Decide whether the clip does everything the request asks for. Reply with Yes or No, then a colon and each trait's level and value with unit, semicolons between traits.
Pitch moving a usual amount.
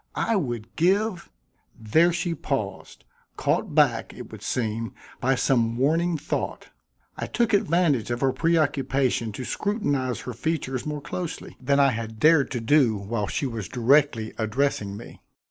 No: wide, 5.9 semitones